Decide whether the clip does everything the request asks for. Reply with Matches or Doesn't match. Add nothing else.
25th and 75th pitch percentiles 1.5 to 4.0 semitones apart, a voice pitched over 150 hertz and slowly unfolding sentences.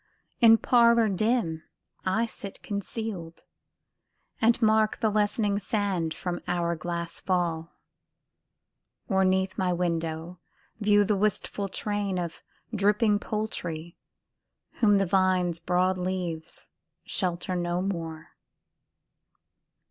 Matches